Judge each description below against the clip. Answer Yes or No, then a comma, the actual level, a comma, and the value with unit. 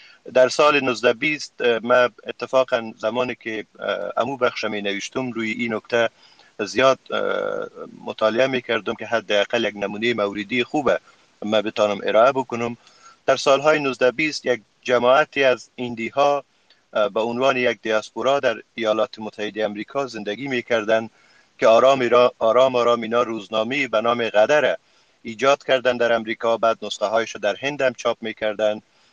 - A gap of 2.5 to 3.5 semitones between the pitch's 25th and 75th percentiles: Yes, average, 3.1 semitones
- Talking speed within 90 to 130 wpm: No, average, 140 wpm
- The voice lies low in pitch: Yes, low, 120 Hz